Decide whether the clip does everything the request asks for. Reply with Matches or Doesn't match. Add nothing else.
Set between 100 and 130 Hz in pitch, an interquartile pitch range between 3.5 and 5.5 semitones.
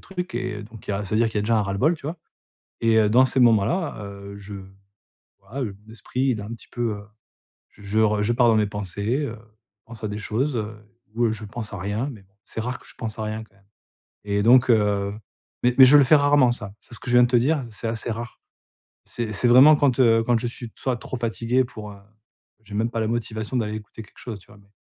Doesn't match